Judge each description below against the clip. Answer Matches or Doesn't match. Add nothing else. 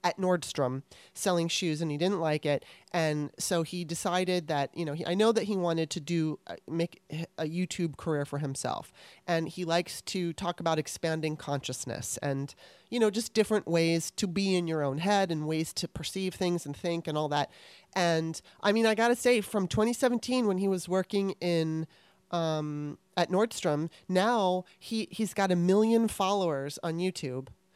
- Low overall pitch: Doesn't match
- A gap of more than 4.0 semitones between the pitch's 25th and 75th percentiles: Doesn't match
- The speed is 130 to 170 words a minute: Doesn't match